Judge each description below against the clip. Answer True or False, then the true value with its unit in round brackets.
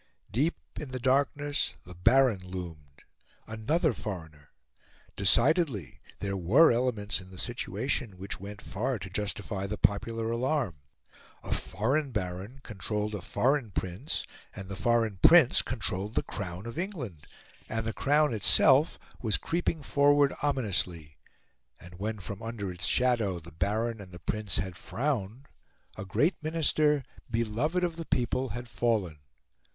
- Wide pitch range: True (6.0 semitones)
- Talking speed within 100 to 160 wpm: True (140 wpm)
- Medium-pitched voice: False (110 Hz)